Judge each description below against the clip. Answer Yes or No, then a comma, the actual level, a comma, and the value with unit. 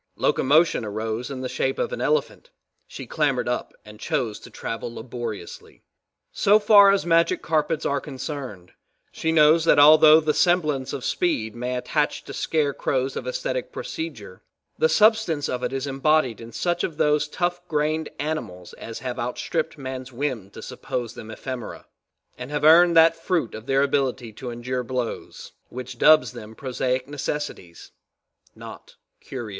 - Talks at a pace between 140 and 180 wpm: Yes, average, 160 wpm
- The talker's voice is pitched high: No, low, 135 Hz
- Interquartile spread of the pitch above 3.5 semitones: Yes, average, 4.5 semitones